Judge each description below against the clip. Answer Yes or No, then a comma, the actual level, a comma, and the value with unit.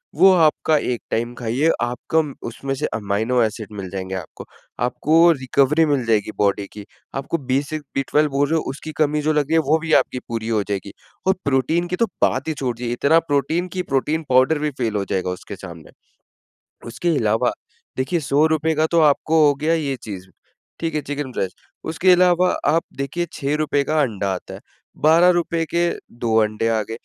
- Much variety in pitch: Yes, wide, 5.8 semitones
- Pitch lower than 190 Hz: Yes, medium, 140 Hz